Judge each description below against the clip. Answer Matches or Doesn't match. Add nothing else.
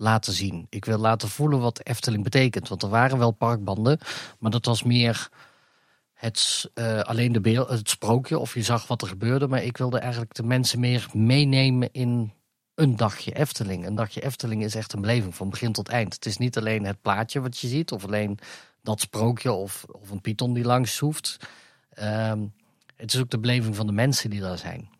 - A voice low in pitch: Matches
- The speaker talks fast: Matches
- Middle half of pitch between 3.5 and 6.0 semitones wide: Doesn't match